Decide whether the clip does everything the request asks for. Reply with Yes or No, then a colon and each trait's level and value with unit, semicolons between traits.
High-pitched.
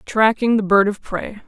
Yes: high, 210 Hz